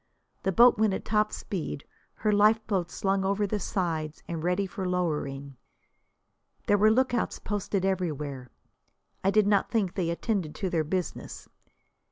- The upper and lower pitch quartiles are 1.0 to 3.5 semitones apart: No, average, 3.9 semitones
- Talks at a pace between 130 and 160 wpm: Yes, average, 150 wpm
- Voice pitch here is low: No, high, 190 Hz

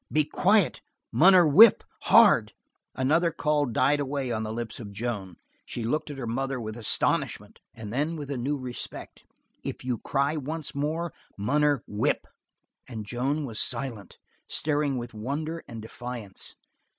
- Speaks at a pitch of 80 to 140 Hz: Yes, low, 135 Hz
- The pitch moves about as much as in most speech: Yes, average, 4.5 semitones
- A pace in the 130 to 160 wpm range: Yes, average, 150 wpm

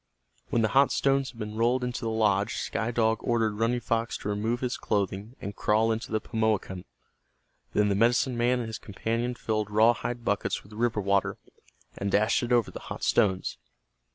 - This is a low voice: Yes, low, 110 Hz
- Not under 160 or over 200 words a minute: Yes, average, 190 wpm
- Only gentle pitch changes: Yes, narrow, 2.3 semitones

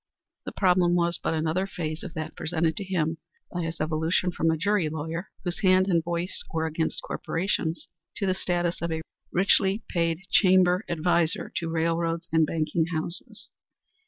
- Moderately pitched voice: Yes, medium, 170 Hz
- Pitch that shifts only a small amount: Yes, narrow, 2.0 semitones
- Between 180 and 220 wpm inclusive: No, average, 165 wpm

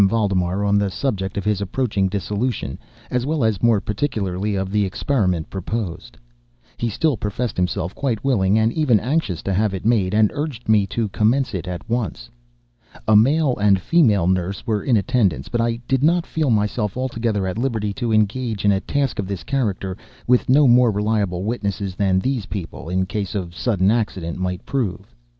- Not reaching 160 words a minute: No, average, 185 wpm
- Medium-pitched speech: No, low, 105 Hz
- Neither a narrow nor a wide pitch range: Yes, average, 4.0 semitones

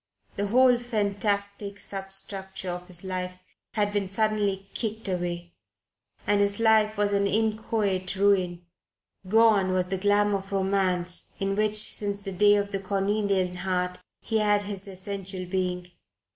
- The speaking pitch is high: Yes, high, 200 Hz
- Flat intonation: Yes, narrow, 1.8 semitones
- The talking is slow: No, average, 145 wpm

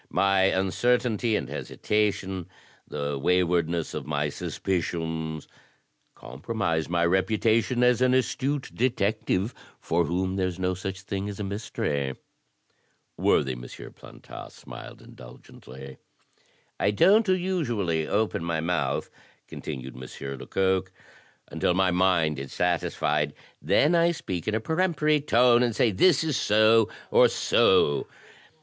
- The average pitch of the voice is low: Yes, very low, 95 Hz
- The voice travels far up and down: Yes, wide, 5.9 semitones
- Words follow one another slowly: Yes, slow, 120 wpm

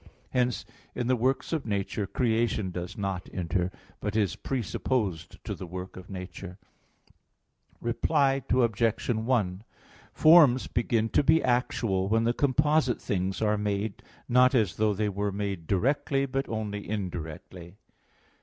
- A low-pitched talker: Yes, low, 110 Hz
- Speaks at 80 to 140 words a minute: Yes, slow, 135 wpm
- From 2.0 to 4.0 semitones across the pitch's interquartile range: No, average, 4.7 semitones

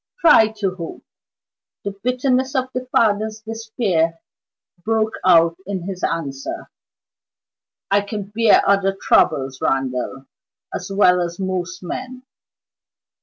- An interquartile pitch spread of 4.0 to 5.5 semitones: Yes, average, 4.5 semitones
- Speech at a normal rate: No, slow, 115 wpm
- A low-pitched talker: No, high, 200 Hz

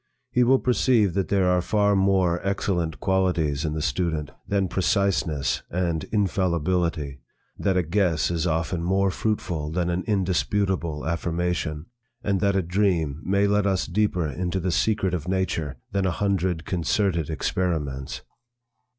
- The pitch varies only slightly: No, average, 3.1 semitones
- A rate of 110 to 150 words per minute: Yes, average, 145 wpm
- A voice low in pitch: Yes, very low, 90 Hz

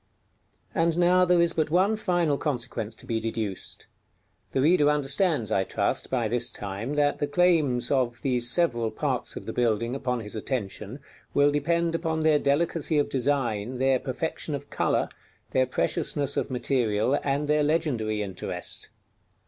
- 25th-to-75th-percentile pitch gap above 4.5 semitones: Yes, average, 5.0 semitones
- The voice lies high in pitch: No, medium, 140 Hz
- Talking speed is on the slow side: No, average, 160 wpm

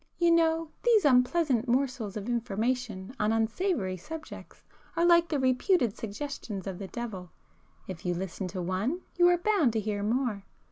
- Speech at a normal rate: Yes, average, 155 wpm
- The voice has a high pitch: Yes, high, 240 Hz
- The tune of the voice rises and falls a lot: Yes, wide, 8.1 semitones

